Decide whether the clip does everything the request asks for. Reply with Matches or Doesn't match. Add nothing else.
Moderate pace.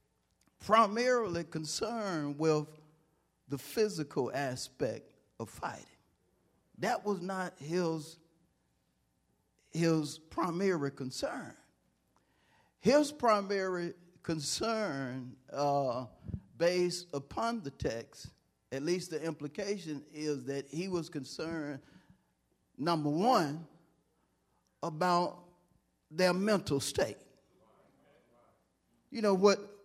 Doesn't match